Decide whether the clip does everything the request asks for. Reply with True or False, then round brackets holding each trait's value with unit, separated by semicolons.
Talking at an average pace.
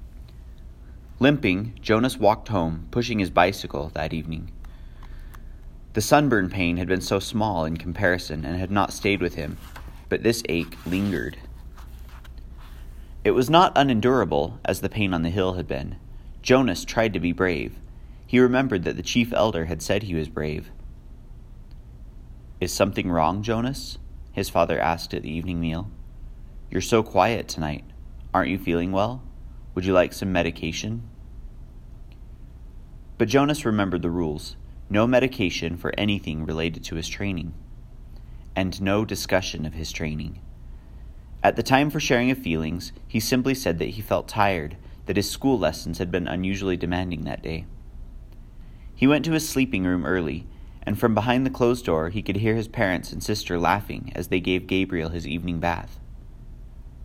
True (160 wpm)